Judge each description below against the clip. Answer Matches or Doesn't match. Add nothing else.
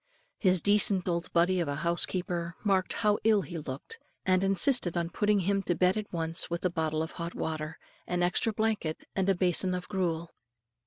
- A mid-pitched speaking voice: Matches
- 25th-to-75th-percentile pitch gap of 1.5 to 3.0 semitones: Matches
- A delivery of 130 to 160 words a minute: Doesn't match